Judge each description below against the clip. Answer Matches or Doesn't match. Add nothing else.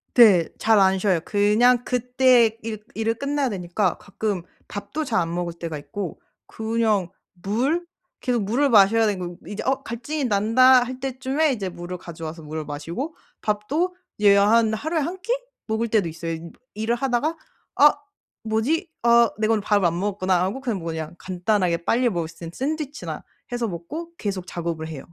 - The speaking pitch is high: Matches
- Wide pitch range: Matches